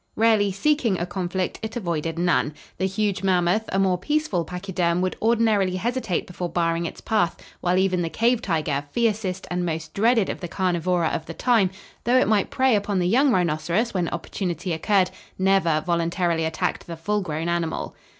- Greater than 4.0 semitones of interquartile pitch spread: No, average, 3.7 semitones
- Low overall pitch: No, medium, 185 Hz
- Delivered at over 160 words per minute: Yes, average, 180 wpm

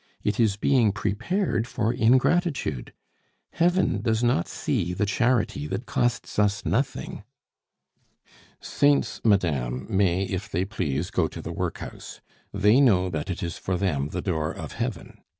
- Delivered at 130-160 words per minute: Yes, average, 150 wpm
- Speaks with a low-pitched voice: Yes, low, 105 Hz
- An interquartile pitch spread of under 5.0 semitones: No, average, 5.3 semitones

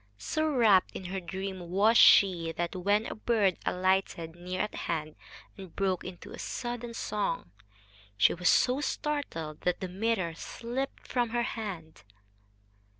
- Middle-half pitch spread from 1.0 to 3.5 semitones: No, average, 4.7 semitones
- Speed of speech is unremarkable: Yes, average, 145 wpm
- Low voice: No, high, 190 Hz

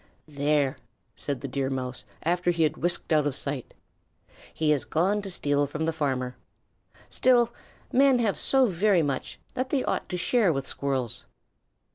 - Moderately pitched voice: Yes, medium, 155 Hz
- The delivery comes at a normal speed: Yes, average, 165 wpm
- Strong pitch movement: Yes, wide, 5.9 semitones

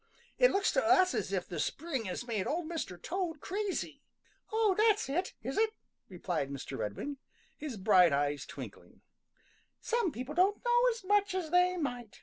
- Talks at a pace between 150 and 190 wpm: Yes, average, 170 wpm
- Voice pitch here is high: Yes, very high, 330 Hz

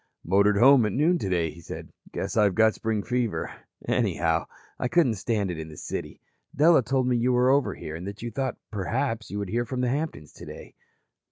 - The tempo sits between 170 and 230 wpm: Yes, fast, 205 wpm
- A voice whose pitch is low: Yes, low, 110 Hz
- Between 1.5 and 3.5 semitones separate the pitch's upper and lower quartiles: No, average, 4.8 semitones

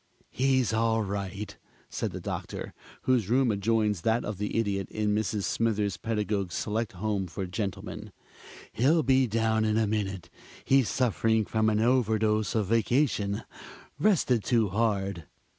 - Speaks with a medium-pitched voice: No, low, 110 Hz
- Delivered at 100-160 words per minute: Yes, average, 140 wpm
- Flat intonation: Yes, narrow, 2.3 semitones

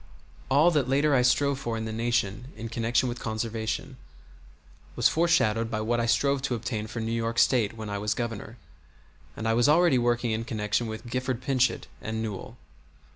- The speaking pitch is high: No, low, 115 Hz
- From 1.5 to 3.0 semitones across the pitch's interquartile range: Yes, narrow, 2.4 semitones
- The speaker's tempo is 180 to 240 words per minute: Yes, average, 185 wpm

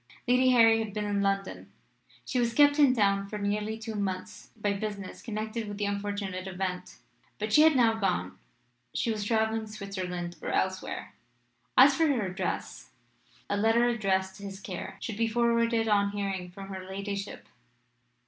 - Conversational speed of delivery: Yes, average, 165 wpm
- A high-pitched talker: Yes, high, 205 Hz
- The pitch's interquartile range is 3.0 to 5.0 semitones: No, narrow, 2.4 semitones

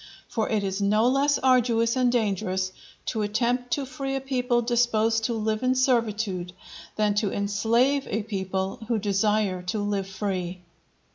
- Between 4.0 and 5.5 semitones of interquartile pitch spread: No, average, 3.6 semitones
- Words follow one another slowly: No, average, 155 wpm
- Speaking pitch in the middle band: No, high, 220 Hz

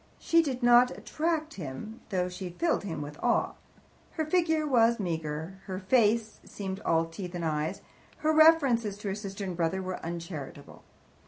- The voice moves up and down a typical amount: No, wide, 6.6 semitones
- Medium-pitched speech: No, high, 200 Hz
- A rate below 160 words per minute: No, average, 165 wpm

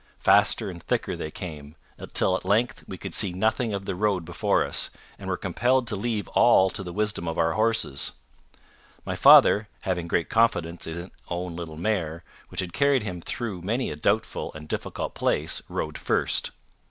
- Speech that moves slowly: No, average, 185 wpm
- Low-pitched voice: Yes, very low, 95 Hz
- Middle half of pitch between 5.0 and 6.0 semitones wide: No, average, 4.2 semitones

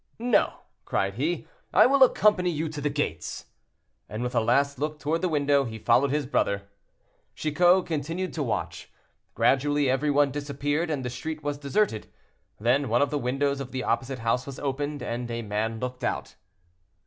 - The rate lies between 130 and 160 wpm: No, average, 180 wpm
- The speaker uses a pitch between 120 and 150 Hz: Yes, medium, 140 Hz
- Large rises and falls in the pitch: No, average, 3.4 semitones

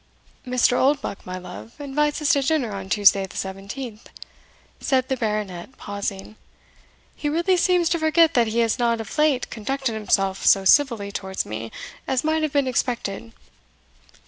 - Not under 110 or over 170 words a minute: Yes, average, 160 wpm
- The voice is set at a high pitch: Yes, high, 235 Hz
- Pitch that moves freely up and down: Yes, wide, 6.2 semitones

